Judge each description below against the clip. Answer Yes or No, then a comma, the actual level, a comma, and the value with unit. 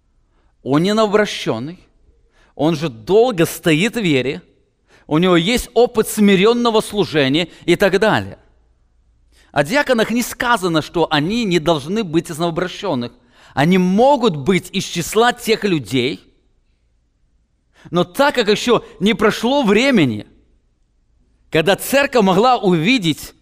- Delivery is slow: Yes, slow, 120 wpm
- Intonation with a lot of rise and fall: Yes, wide, 7.1 semitones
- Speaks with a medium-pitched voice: Yes, medium, 180 Hz